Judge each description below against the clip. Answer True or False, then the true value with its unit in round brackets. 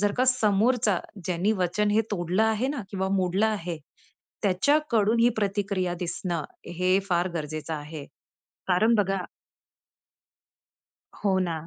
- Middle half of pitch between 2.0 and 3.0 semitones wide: False (3.5 semitones)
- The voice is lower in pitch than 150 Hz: False (195 Hz)